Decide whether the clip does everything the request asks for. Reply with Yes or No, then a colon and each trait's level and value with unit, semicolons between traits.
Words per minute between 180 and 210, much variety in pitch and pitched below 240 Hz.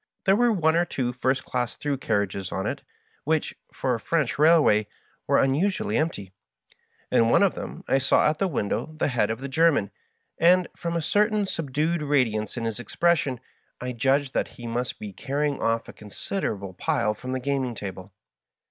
Yes: average, 190 wpm; wide, 6.0 semitones; low, 135 Hz